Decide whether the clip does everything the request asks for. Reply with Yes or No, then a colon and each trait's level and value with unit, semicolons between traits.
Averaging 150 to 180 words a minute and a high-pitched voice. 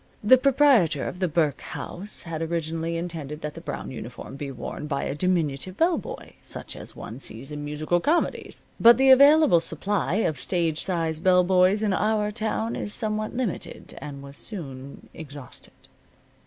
No: average, 170 wpm; medium, 170 Hz